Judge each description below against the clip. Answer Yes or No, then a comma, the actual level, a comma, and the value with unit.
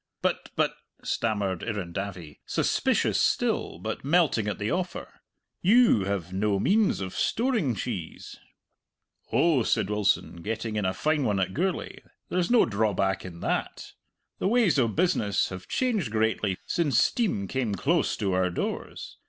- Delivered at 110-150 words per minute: Yes, average, 145 wpm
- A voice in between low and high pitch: No, low, 110 Hz